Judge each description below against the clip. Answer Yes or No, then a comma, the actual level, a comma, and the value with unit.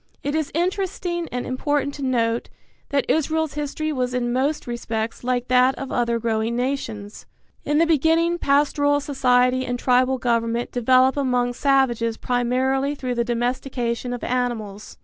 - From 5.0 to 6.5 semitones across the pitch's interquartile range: No, average, 3.0 semitones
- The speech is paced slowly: No, average, 150 wpm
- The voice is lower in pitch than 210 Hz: No, very high, 255 Hz